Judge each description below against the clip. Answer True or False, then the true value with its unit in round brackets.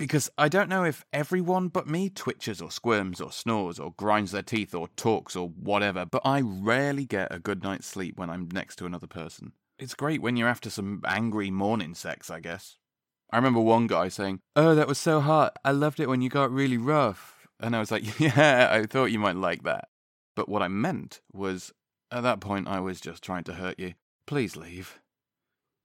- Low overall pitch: True (110 Hz)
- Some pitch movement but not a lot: False (6.6 semitones)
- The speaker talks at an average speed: False (215 wpm)